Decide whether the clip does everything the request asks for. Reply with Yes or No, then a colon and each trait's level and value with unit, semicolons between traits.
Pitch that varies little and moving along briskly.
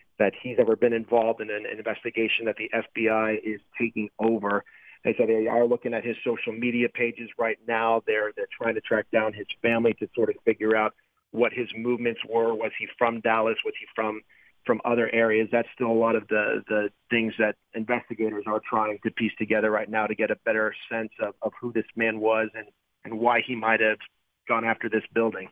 Yes: narrow, 1.2 semitones; fast, 215 wpm